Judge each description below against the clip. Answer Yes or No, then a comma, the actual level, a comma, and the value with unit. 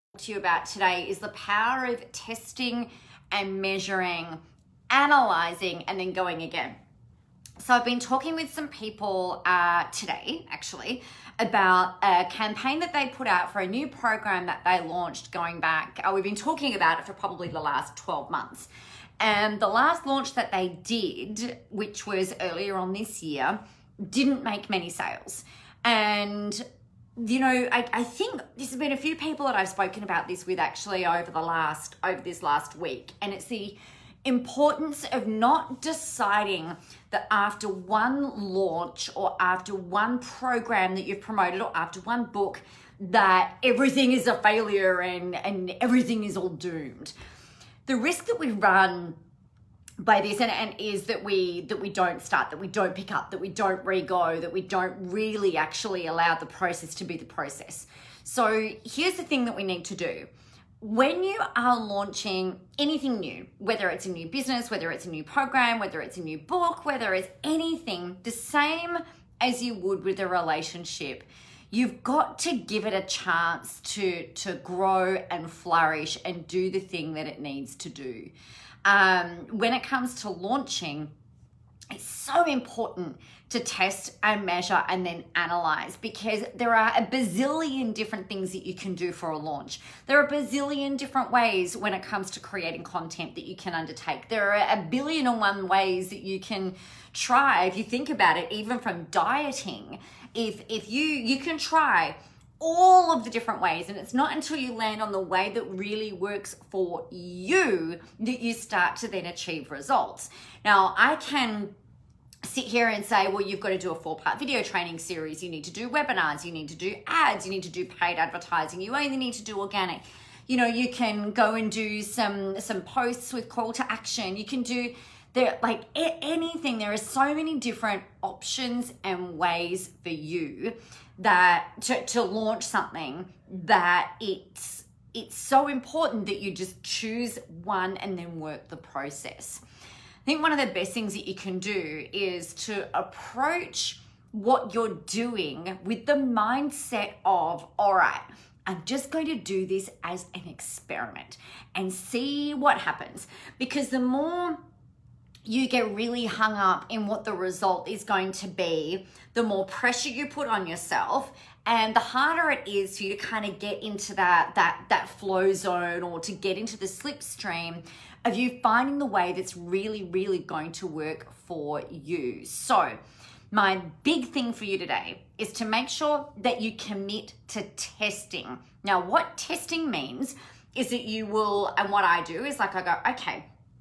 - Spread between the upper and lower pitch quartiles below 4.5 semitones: No, average, 5.1 semitones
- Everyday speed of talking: Yes, average, 180 wpm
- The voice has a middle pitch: No, high, 205 Hz